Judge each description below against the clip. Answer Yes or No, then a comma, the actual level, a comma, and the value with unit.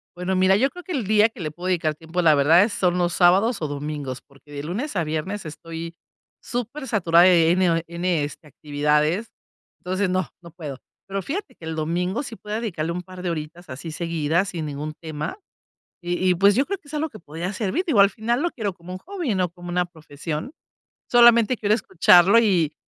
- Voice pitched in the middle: Yes, medium, 180 Hz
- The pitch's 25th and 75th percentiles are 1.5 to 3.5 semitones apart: No, average, 4.7 semitones